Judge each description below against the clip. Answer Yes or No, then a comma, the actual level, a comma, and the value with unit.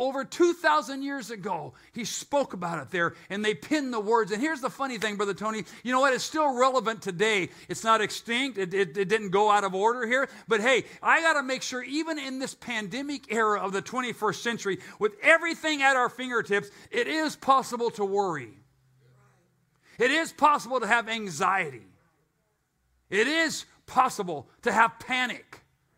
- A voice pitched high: Yes, high, 230 Hz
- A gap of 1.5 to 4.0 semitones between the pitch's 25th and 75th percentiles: No, average, 5.0 semitones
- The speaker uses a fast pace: No, average, 180 wpm